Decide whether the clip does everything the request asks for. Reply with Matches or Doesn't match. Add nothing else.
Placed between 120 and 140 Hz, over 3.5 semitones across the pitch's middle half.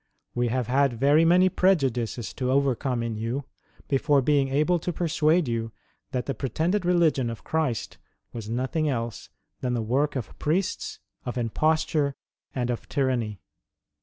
Matches